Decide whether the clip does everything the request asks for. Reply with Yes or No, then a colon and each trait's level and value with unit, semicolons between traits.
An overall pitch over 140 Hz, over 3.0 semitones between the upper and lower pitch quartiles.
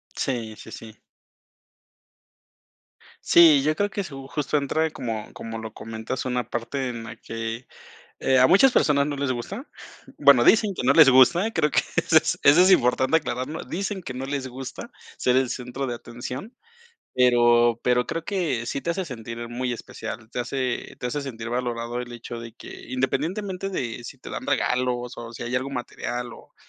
No: low, 125 Hz; average, 3.7 semitones